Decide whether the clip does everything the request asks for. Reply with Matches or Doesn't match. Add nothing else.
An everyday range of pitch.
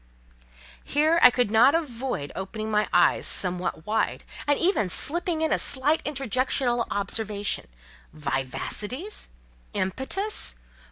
Doesn't match